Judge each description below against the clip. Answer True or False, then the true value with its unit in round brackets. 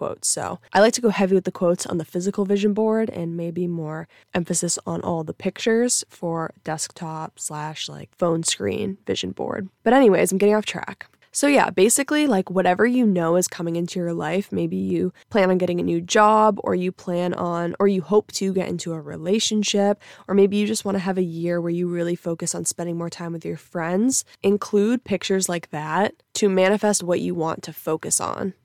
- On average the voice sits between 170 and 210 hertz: True (185 Hz)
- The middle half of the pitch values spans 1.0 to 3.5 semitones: True (3.2 semitones)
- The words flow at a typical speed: False (210 wpm)